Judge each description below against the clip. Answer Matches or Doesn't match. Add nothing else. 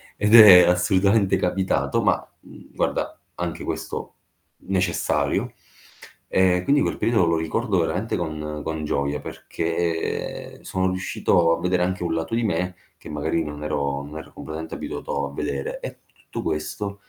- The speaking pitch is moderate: Doesn't match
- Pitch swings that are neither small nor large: Matches